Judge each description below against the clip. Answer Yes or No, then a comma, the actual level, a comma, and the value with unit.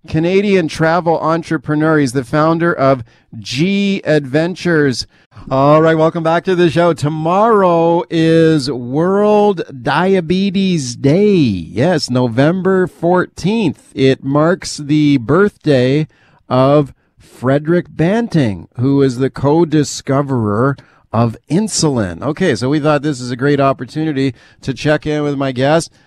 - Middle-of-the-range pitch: Yes, medium, 150 Hz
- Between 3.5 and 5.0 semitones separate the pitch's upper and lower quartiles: Yes, average, 3.9 semitones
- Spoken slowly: Yes, slow, 120 wpm